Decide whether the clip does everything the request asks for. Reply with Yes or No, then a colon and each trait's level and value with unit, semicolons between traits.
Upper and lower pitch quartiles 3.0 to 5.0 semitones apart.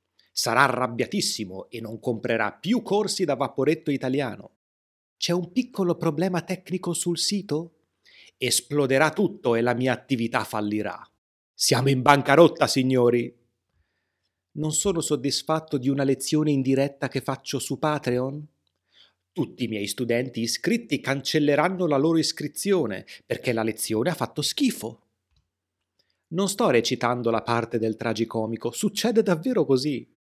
No: wide, 5.6 semitones